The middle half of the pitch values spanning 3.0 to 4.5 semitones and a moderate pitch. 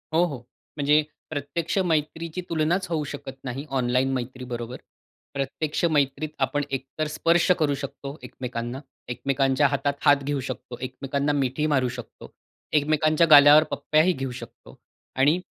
No: narrow, 2.6 semitones; medium, 145 Hz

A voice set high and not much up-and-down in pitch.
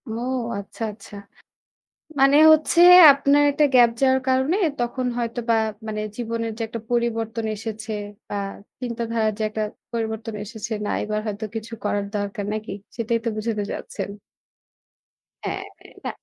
Yes: high, 230 Hz; narrow, 1.9 semitones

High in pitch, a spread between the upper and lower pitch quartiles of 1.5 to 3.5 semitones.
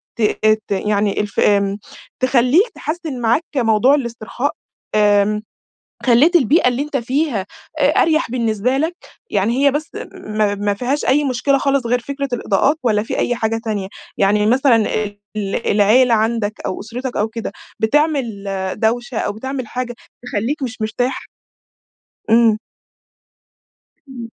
No: high, 235 Hz; average, 4.1 semitones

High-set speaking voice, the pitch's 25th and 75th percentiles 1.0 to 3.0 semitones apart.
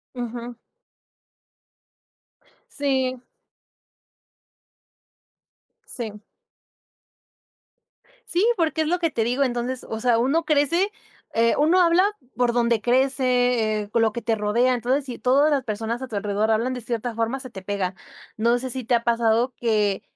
Yes: high, 245 Hz; average, 2.7 semitones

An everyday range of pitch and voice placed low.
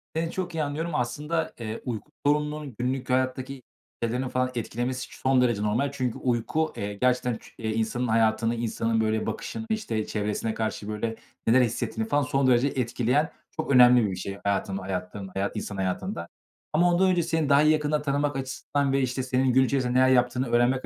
Yes: average, 4.0 semitones; low, 125 Hz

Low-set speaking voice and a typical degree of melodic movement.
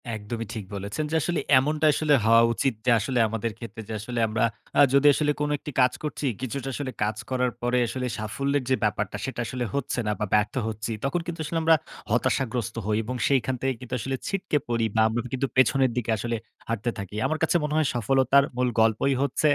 Yes: low, 125 Hz; average, 3.7 semitones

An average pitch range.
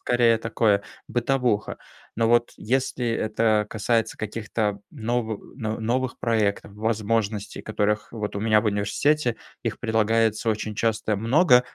No: narrow, 1.9 semitones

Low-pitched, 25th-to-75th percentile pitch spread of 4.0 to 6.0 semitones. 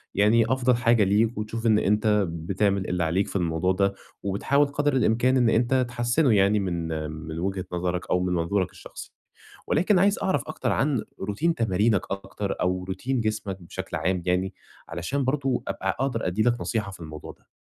Yes: low, 100 Hz; average, 4.7 semitones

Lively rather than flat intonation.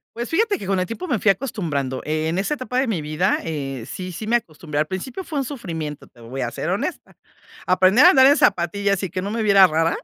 Yes: wide, 7.2 semitones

